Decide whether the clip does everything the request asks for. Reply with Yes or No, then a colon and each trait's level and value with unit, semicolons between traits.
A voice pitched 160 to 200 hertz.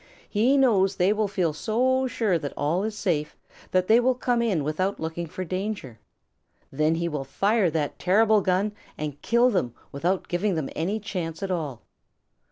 Yes: medium, 185 Hz